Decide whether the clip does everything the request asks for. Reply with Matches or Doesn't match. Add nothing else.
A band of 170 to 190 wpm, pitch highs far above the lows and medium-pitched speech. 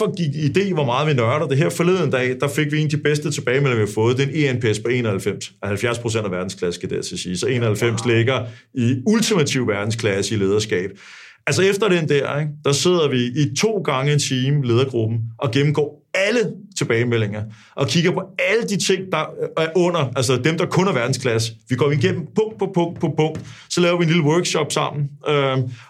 Doesn't match